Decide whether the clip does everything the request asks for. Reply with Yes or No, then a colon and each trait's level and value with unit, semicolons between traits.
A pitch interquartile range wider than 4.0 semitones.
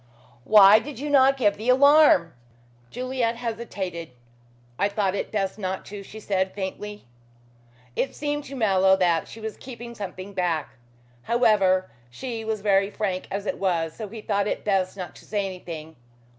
No: average, 3.6 semitones